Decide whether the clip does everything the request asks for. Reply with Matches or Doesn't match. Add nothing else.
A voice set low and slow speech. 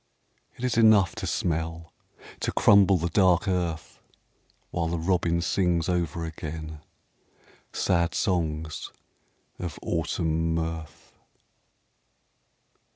Matches